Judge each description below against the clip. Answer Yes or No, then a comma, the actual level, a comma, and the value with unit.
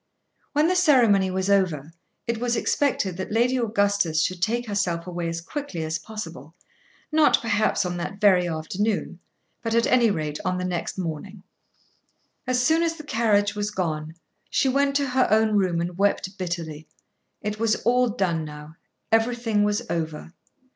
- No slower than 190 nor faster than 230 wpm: No, average, 165 wpm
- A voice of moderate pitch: No, high, 200 Hz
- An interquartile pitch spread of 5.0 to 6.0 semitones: Yes, wide, 5.4 semitones